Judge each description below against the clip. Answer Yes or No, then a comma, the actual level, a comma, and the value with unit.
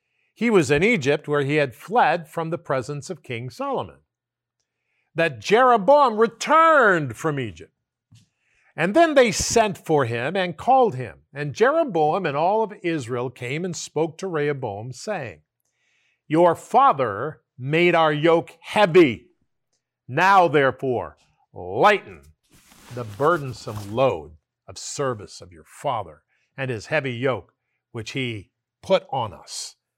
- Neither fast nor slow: No, slow, 130 wpm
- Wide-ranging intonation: Yes, wide, 6.1 semitones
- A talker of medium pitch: Yes, medium, 150 Hz